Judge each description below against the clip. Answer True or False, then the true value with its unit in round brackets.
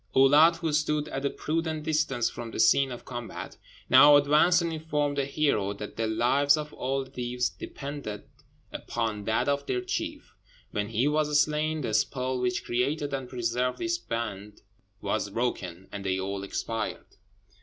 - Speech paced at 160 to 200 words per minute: True (165 wpm)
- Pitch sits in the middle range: False (130 Hz)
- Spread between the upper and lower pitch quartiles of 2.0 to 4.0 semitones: False (4.6 semitones)